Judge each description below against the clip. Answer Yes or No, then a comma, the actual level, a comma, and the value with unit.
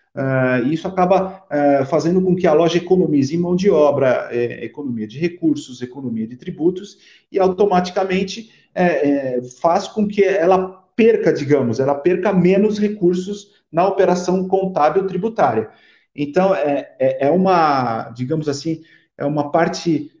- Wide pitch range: No, average, 4.9 semitones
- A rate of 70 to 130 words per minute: No, average, 145 wpm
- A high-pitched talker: No, medium, 175 Hz